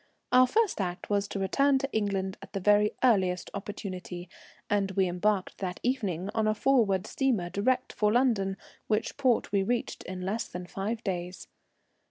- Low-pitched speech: No, high, 200 Hz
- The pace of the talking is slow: No, average, 170 wpm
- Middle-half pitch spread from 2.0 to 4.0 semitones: Yes, average, 3.5 semitones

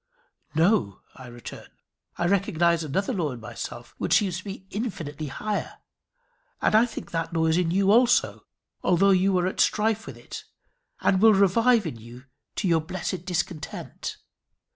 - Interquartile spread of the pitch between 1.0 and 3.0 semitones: No, average, 3.8 semitones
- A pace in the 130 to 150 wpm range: No, average, 165 wpm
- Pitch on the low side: No, medium, 180 Hz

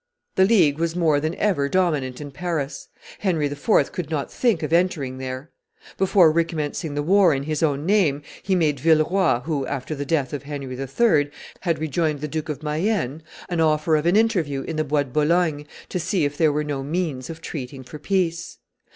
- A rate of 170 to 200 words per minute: Yes, average, 195 wpm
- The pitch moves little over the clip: No, average, 3.3 semitones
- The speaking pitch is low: No, medium, 155 Hz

